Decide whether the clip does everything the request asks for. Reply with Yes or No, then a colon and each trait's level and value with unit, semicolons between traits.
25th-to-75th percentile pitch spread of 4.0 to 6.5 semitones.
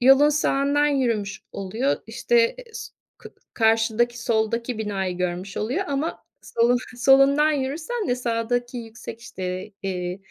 Yes: average, 4.5 semitones